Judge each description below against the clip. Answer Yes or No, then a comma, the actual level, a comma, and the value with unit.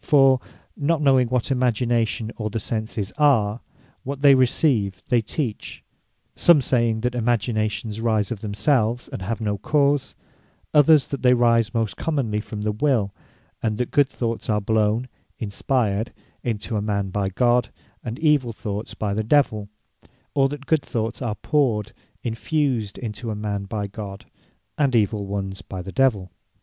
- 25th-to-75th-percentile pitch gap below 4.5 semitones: Yes, average, 3.7 semitones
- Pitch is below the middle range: Yes, low, 115 Hz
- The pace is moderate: Yes, average, 160 wpm